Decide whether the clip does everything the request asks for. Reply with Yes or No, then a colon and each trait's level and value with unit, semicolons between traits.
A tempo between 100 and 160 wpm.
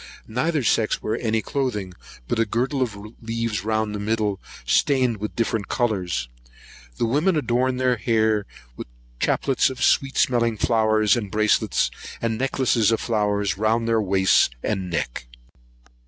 Yes: average, 145 wpm